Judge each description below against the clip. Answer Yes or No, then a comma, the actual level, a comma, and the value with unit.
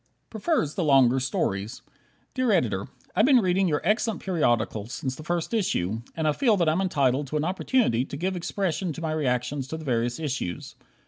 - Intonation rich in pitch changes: Yes, wide, 6.8 semitones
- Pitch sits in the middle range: Yes, medium, 155 Hz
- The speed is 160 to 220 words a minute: Yes, average, 190 wpm